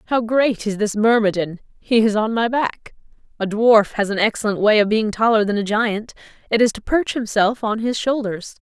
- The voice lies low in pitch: No, high, 220 Hz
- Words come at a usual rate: No, fast, 210 wpm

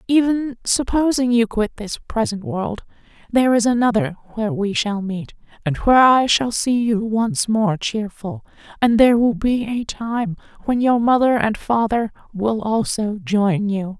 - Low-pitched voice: No, high, 225 Hz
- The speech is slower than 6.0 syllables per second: Yes, 4.3 syllables/s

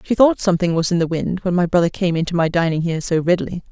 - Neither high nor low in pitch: Yes, medium, 175 Hz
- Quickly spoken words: Yes, fast, 275 wpm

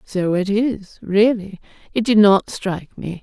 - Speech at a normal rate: Yes, average, 165 wpm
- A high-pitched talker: Yes, high, 200 Hz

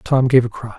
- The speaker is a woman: No, male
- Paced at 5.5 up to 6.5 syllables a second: Yes, 6.1 syllables/s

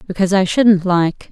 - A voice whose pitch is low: No, high, 190 Hz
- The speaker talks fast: No, average, 180 wpm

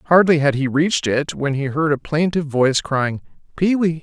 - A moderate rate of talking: No, fast, 210 wpm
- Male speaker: Yes, male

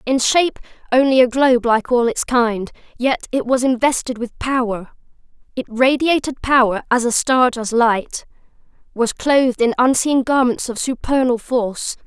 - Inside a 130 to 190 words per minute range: Yes, average, 155 wpm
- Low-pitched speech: No, very high, 250 Hz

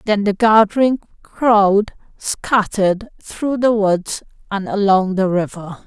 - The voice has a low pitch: No, high, 205 Hz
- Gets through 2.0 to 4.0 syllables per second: Yes, 3.6 syllables/s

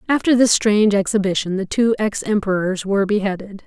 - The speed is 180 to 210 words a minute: No, average, 165 wpm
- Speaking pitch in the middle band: No, high, 205 Hz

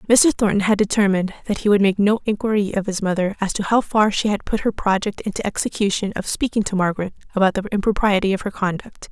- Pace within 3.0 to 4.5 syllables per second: No, 6.4 syllables/s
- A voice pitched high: Yes, high, 200 Hz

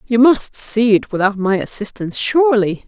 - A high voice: Yes, high, 220 Hz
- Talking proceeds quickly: No, average, 165 wpm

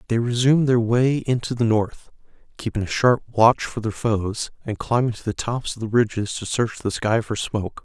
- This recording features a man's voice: Yes, male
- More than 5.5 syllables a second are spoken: No, 5.1 syllables/s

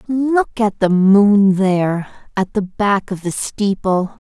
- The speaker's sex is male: No, female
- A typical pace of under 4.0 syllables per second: Yes, 3.5 syllables/s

